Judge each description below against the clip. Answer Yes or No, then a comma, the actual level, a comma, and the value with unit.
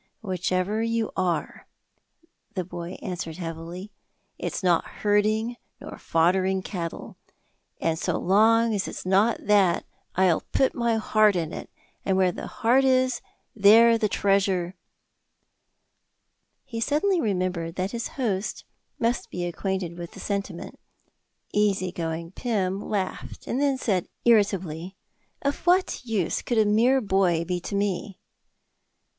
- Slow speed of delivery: Yes, slow, 130 wpm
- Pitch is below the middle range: No, high, 195 Hz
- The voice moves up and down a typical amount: Yes, average, 3.9 semitones